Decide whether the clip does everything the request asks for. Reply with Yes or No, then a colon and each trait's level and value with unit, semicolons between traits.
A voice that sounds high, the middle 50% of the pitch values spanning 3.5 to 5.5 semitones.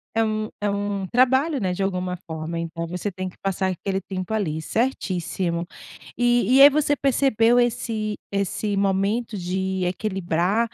Yes: high, 195 Hz; average, 3.9 semitones